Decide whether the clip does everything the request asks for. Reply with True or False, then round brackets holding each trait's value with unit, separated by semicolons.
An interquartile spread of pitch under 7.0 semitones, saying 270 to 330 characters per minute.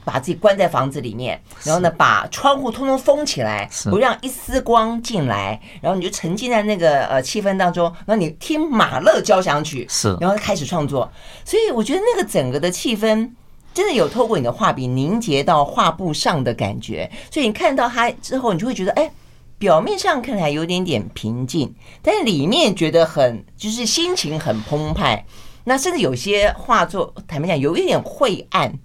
False (7.8 semitones; 295 characters per minute)